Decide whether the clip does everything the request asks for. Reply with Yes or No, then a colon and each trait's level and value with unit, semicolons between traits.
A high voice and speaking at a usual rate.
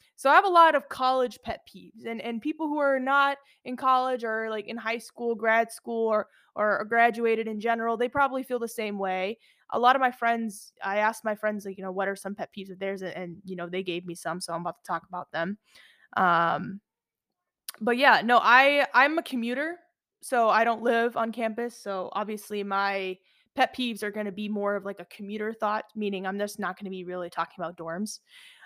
No: high, 220 Hz; fast, 220 wpm